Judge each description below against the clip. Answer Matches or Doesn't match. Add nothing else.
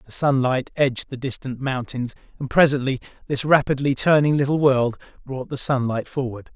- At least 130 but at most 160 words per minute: Matches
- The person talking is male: Matches